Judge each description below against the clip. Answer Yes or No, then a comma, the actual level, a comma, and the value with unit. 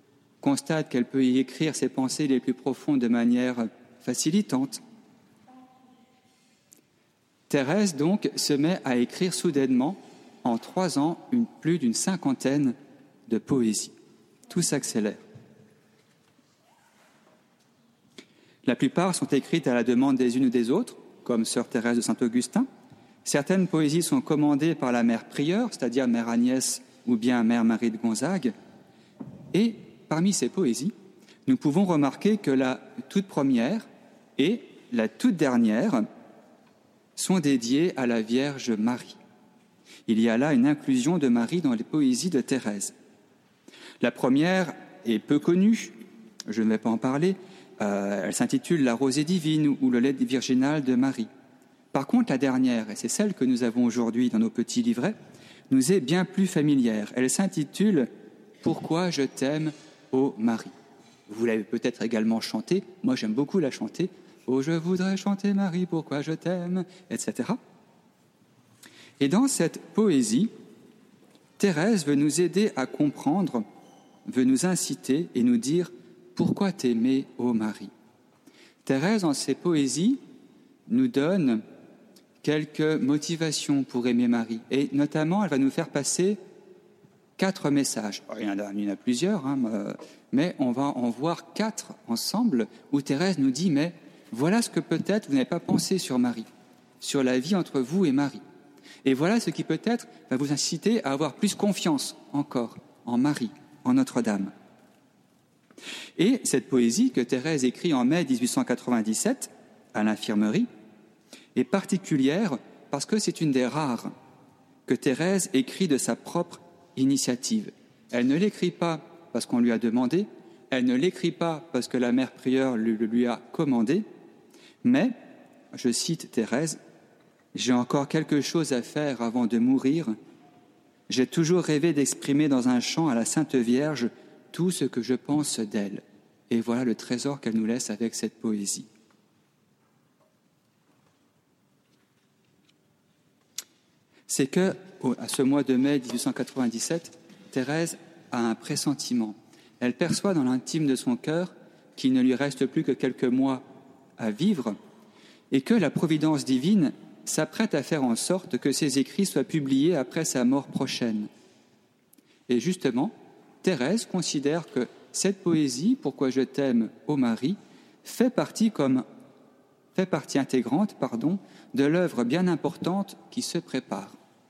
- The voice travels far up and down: Yes, wide, 7.7 semitones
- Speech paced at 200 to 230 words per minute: No, slow, 145 wpm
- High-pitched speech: No, medium, 150 Hz